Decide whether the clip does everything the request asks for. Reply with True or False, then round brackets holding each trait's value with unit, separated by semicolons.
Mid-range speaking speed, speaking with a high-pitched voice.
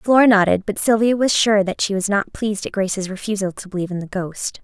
False (245 wpm; 205 Hz)